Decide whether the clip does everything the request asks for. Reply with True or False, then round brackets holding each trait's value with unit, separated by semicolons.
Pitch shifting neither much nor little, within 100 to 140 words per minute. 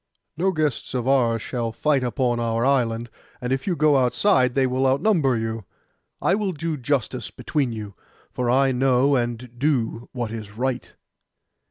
False (3.0 semitones; 165 wpm)